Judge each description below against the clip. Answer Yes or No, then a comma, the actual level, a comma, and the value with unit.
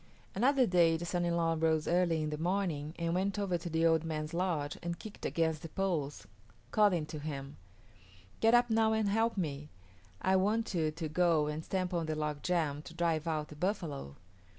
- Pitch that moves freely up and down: No, average, 3.5 semitones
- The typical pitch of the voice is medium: Yes, medium, 165 Hz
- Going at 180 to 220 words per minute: Yes, average, 200 wpm